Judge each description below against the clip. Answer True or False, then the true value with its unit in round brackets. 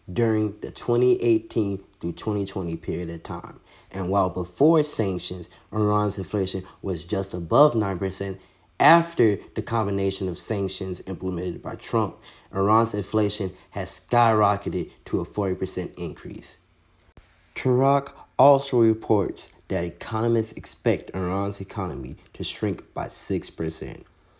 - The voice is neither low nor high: False (95 Hz)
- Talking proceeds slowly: True (115 wpm)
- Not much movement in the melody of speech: False (3.2 semitones)